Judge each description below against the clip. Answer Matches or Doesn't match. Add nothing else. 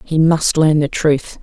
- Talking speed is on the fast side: Matches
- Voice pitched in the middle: Matches